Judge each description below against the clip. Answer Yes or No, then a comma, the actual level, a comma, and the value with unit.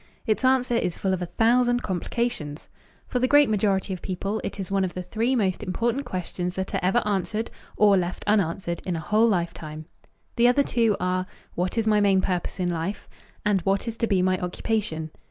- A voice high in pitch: Yes, high, 195 Hz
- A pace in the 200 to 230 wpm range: Yes, fast, 205 wpm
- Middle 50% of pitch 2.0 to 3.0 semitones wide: No, average, 3.9 semitones